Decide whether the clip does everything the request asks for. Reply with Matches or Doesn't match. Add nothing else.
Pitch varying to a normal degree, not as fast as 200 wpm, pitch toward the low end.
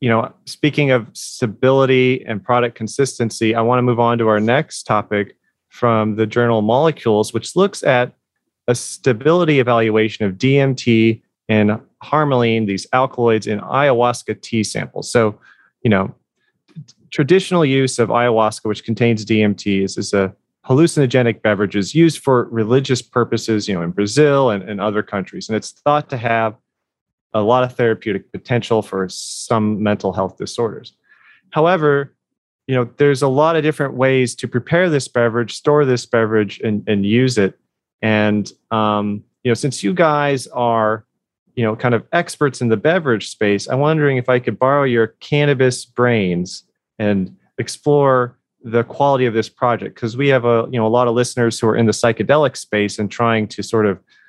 Matches